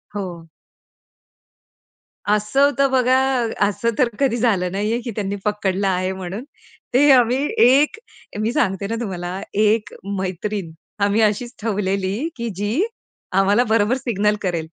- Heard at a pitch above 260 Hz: No, high, 210 Hz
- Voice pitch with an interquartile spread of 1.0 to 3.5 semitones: No, average, 4.0 semitones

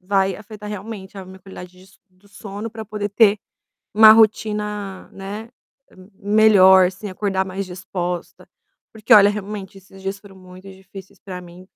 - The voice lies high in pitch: Yes, high, 195 Hz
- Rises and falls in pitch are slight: Yes, narrow, 1.8 semitones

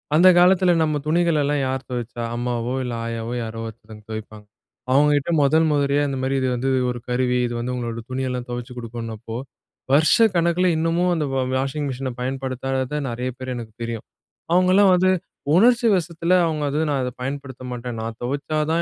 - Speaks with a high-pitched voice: No, low, 130 Hz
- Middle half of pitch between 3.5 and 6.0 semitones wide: Yes, average, 4.6 semitones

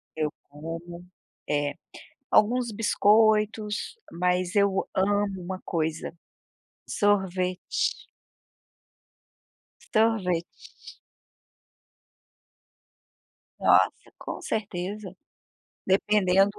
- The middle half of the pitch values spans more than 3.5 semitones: No, average, 3.0 semitones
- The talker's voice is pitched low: No, high, 190 Hz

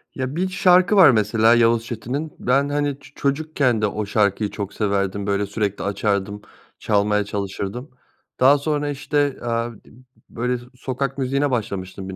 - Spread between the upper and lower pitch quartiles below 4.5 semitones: No, wide, 5.4 semitones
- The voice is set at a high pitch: No, low, 115 Hz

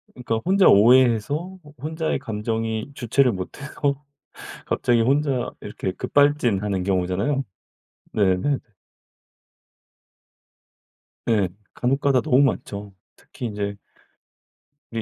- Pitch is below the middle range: Yes, low, 120 Hz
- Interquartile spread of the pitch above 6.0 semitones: No, average, 5.2 semitones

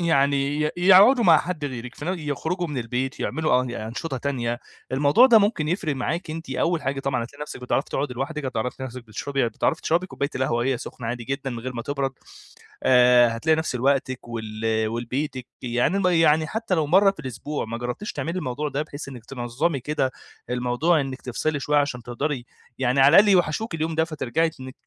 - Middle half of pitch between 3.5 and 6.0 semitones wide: Yes, average, 4.4 semitones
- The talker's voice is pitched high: No, medium, 140 Hz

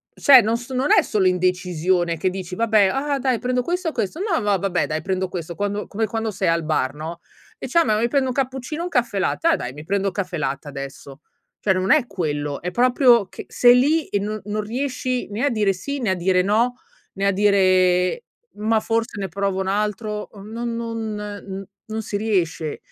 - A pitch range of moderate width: Yes, average, 4.6 semitones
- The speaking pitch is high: Yes, high, 205 Hz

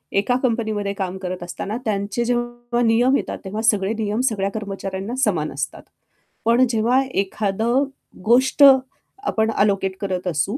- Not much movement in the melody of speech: No, average, 3.5 semitones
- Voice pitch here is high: Yes, high, 215 Hz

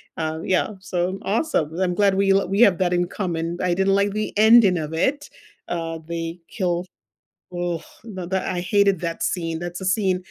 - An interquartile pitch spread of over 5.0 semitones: No, narrow, 2.4 semitones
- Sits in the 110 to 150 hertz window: No, medium, 180 Hz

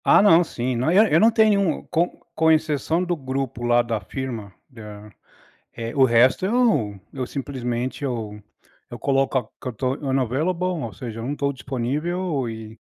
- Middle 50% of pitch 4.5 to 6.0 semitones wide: Yes, average, 5.3 semitones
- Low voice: Yes, low, 130 Hz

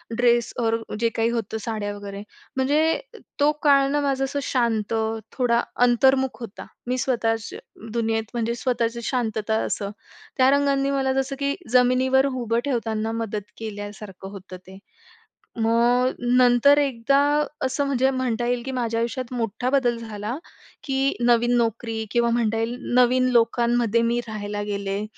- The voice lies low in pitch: No, high, 235 Hz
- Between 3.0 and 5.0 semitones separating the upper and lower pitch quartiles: No, narrow, 2.6 semitones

